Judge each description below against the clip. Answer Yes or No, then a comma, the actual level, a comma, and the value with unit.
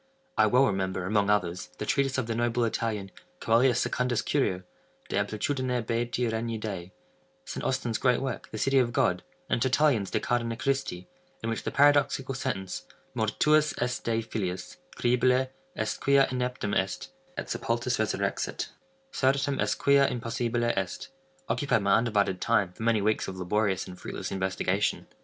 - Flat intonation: No, average, 4.1 semitones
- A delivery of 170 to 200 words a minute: No, average, 155 wpm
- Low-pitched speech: Yes, low, 115 Hz